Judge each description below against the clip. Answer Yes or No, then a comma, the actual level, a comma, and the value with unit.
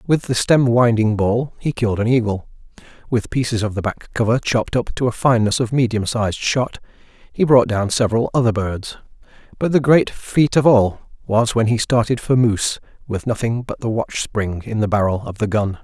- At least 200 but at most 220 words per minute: Yes, fast, 205 wpm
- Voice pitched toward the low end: Yes, low, 115 Hz